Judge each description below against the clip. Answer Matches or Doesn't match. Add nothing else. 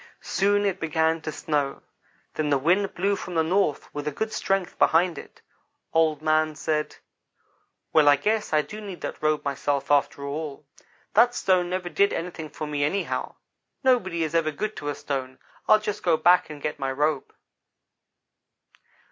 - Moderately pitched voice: Matches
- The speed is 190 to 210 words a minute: Doesn't match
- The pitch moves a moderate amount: Matches